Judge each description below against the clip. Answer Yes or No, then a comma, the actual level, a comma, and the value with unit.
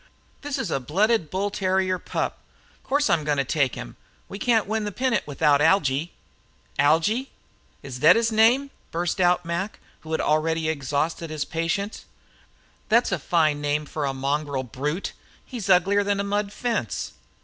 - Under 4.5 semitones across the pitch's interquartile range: No, wide, 5.5 semitones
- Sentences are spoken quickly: No, average, 160 wpm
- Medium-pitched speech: Yes, medium, 170 Hz